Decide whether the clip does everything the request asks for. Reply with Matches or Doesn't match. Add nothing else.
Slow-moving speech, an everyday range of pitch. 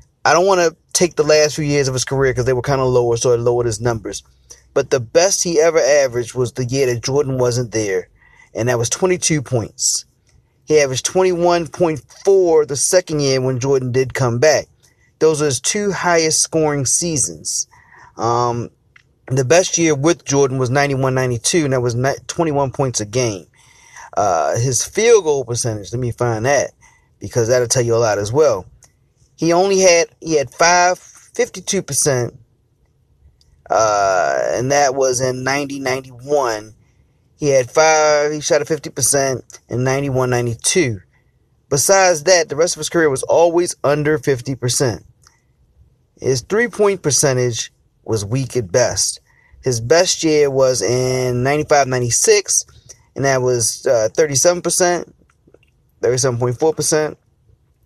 Doesn't match